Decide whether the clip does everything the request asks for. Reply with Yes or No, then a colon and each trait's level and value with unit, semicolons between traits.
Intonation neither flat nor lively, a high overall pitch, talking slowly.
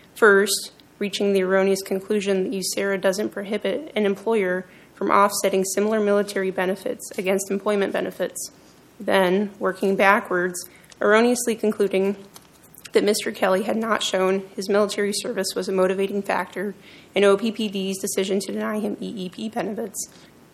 No: narrow, 1.4 semitones; high, 200 Hz; slow, 130 wpm